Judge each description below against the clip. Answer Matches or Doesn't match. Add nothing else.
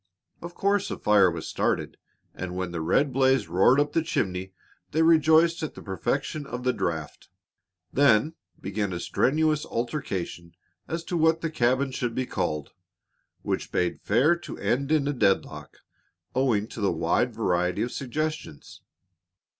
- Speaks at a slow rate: Doesn't match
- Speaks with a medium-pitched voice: Doesn't match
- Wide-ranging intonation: Matches